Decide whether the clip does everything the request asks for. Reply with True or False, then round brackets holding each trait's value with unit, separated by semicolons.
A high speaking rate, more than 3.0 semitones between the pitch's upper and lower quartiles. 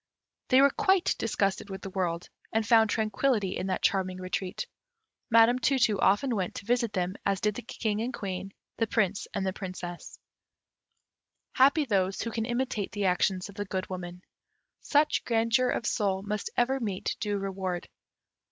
False (170 wpm; 3.6 semitones)